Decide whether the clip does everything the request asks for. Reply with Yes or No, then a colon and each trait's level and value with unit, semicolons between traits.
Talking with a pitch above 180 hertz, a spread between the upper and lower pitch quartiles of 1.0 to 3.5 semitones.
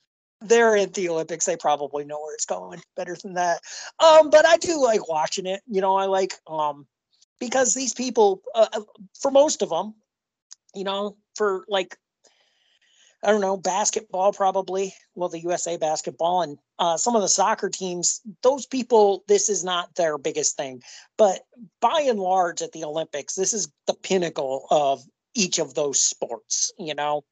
No: high, 190 Hz; average, 4.8 semitones